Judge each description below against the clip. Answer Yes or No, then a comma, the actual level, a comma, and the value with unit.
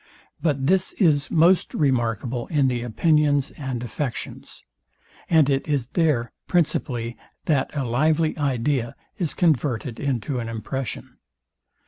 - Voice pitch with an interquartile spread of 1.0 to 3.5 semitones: No, average, 4.2 semitones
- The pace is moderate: No, slow, 120 wpm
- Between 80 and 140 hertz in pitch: Yes, low, 135 Hz